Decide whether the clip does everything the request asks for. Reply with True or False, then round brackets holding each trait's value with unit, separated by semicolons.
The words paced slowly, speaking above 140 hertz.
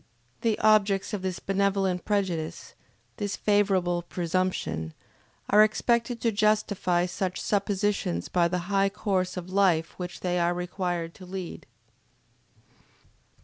True (120 wpm; 190 Hz)